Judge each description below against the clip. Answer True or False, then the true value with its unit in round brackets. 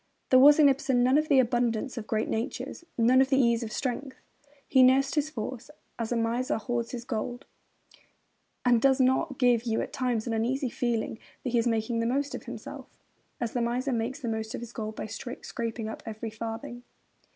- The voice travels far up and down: False (2.4 semitones)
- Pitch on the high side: True (240 Hz)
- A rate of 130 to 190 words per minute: False (205 wpm)